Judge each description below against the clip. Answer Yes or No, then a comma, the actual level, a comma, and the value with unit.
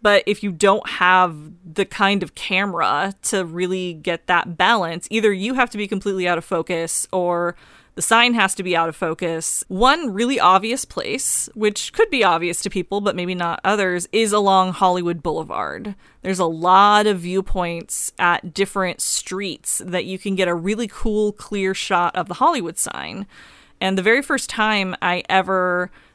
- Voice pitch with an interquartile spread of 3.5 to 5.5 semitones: No, average, 2.7 semitones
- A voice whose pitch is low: No, high, 190 Hz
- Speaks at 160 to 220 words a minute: Yes, average, 180 wpm